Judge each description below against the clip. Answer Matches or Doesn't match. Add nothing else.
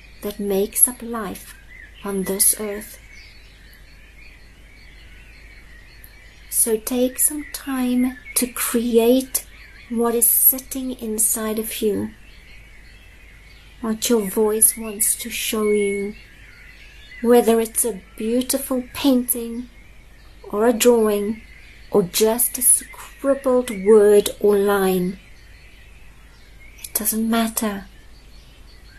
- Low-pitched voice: Doesn't match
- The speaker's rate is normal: Doesn't match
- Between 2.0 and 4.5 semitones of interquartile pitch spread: Matches